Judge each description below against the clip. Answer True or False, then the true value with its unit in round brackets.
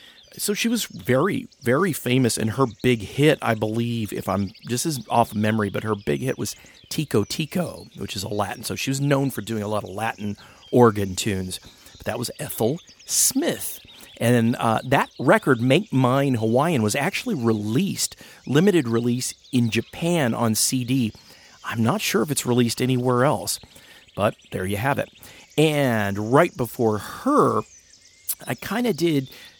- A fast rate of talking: False (170 wpm)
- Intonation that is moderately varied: True (4.2 semitones)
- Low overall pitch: True (120 Hz)